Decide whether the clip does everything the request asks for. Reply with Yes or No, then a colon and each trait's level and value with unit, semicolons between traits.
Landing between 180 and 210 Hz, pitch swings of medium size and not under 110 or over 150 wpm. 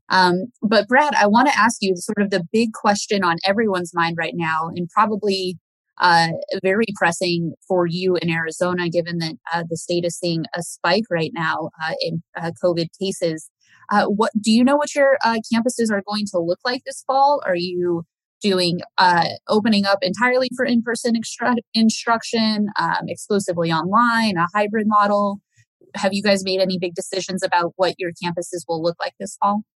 No: high, 190 Hz; average, 4.2 semitones; average, 190 wpm